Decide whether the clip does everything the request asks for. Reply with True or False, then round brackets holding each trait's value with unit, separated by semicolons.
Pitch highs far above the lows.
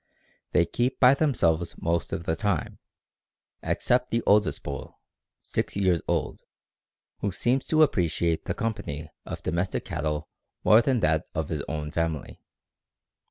True (6.5 semitones)